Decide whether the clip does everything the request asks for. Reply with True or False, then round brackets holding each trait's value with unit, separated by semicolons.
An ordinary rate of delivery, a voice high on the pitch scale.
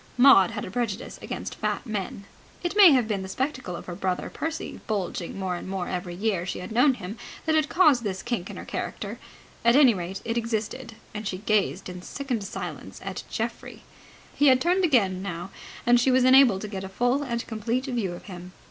False (210 wpm; 220 Hz)